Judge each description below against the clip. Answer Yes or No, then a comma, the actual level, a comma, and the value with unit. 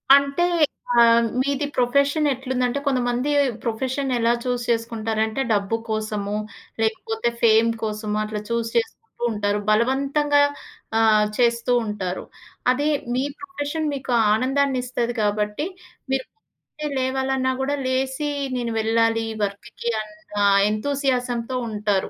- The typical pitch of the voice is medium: No, high, 240 Hz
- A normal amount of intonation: Yes, average, 3.4 semitones